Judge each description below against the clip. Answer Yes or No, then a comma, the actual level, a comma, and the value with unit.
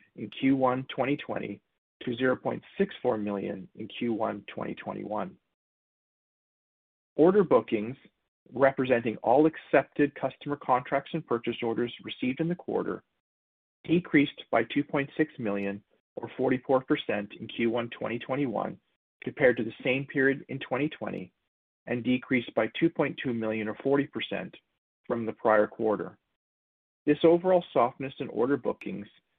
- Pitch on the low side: Yes, low, 125 Hz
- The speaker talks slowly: Yes, slow, 115 wpm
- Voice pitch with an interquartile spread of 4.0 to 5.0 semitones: Yes, average, 4.3 semitones